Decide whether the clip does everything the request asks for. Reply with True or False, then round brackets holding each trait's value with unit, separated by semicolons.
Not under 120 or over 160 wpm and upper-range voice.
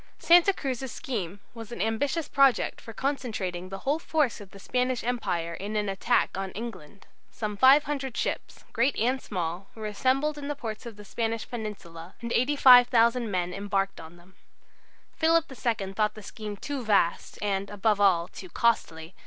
False (175 wpm; 220 Hz)